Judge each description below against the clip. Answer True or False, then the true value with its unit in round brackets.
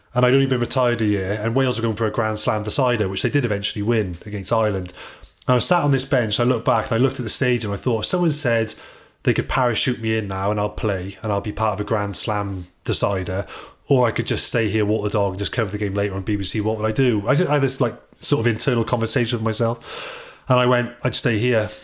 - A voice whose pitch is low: True (115 Hz)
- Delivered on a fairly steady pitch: False (3.1 semitones)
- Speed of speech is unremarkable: False (280 wpm)